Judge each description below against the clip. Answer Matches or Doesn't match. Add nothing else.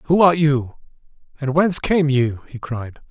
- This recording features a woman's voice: Doesn't match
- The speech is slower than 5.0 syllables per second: Matches